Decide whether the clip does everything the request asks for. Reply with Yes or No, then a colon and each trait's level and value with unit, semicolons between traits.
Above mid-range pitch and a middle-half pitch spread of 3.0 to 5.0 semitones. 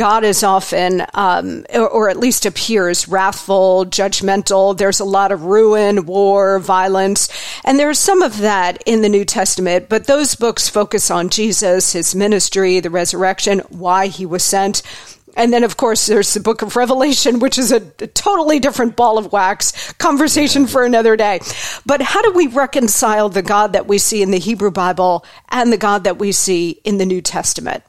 Yes: high, 205 Hz; average, 3.8 semitones